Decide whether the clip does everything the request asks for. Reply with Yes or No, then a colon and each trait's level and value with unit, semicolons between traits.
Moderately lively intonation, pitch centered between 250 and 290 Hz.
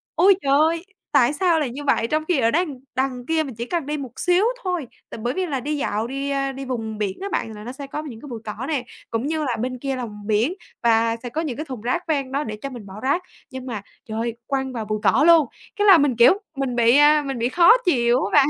Yes: average, 4.3 semitones; very high, 270 Hz